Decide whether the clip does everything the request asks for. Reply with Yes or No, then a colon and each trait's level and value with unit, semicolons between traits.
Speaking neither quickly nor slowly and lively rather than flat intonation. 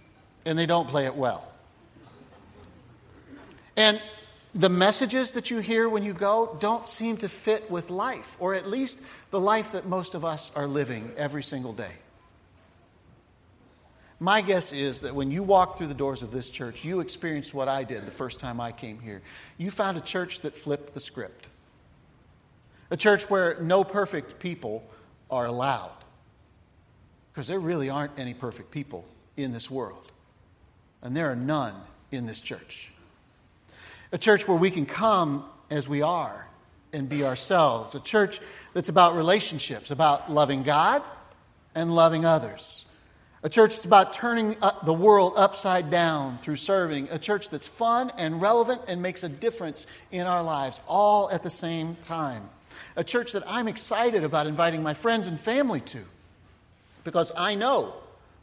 Yes: average, 165 wpm; wide, 7.4 semitones